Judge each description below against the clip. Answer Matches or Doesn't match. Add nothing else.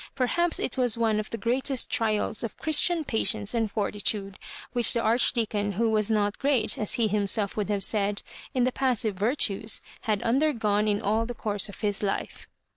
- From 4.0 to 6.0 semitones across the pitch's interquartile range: Doesn't match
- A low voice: Doesn't match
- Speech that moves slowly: Doesn't match